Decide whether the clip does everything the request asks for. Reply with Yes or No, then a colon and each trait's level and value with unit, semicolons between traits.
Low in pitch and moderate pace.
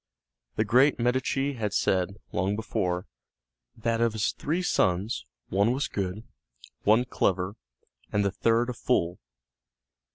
No: low, 110 Hz; slow, 130 wpm